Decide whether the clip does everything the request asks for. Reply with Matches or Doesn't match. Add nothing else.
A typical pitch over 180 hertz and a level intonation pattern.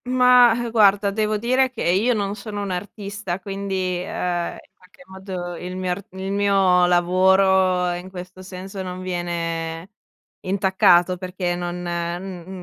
Matches